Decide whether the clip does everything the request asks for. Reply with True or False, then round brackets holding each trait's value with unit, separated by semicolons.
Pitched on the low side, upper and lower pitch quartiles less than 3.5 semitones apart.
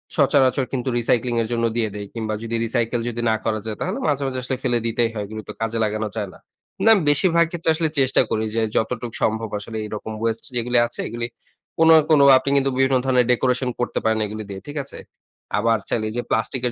True (120 Hz; 2.9 semitones)